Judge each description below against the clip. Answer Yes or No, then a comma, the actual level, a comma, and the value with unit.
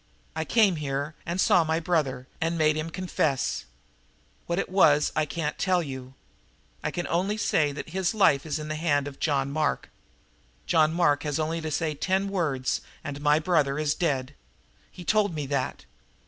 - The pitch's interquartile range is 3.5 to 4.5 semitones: No, average, 3.1 semitones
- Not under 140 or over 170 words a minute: No, average, 180 wpm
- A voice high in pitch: No, medium, 155 Hz